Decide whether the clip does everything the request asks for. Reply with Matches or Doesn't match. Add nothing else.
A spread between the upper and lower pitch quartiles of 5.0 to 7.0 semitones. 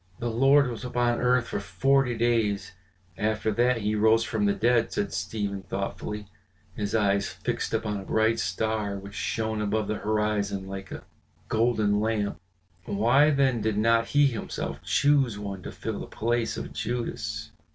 Doesn't match